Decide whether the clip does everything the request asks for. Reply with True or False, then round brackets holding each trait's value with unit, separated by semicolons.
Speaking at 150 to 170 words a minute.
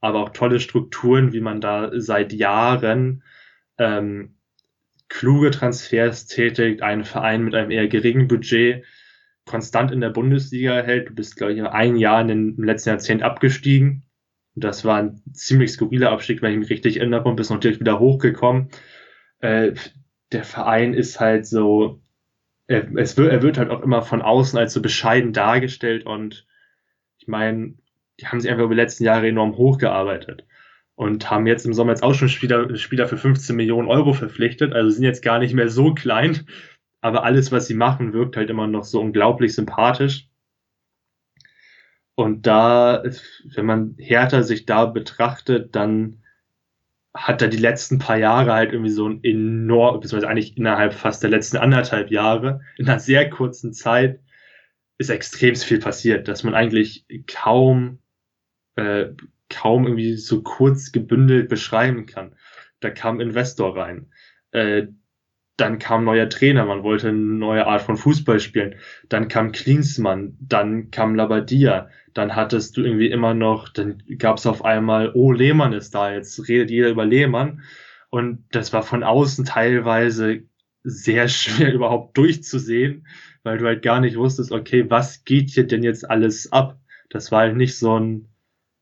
True (165 wpm)